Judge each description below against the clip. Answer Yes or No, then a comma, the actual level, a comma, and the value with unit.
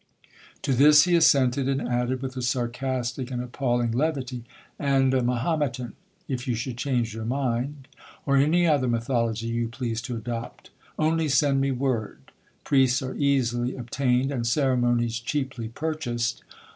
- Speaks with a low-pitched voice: Yes, low, 130 Hz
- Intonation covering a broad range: No, narrow, 2.4 semitones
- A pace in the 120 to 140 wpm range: Yes, slow, 135 wpm